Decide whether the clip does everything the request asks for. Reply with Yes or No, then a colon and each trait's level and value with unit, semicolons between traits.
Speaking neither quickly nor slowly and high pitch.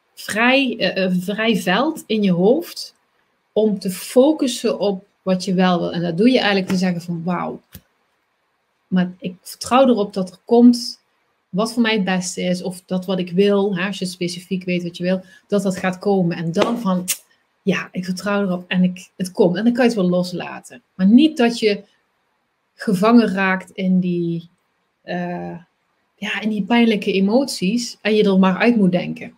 Yes: average, 190 wpm; high, 195 Hz